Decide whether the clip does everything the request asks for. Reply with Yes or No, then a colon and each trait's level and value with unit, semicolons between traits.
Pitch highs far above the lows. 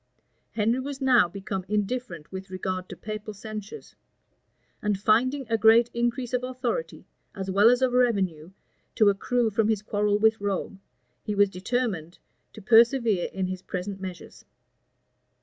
No: average, 3.7 semitones